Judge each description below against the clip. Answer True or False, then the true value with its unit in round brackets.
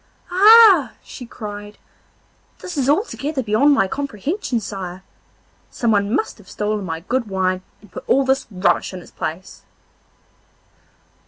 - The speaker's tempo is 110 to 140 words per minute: True (135 wpm)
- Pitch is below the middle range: False (225 Hz)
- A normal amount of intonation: False (6.5 semitones)